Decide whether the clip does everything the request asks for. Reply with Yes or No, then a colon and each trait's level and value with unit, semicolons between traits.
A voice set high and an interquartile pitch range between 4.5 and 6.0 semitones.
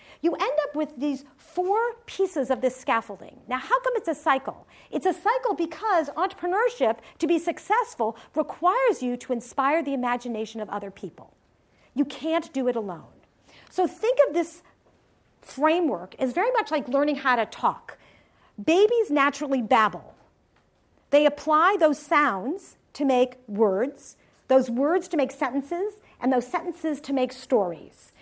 Yes: very high, 295 Hz; average, 5.1 semitones